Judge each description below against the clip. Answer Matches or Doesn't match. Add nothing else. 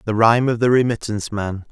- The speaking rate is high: Matches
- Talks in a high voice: Doesn't match